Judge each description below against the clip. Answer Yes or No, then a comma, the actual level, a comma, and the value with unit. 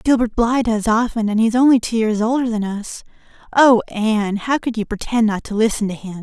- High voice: Yes, high, 225 Hz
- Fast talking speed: Yes, fast, 220 wpm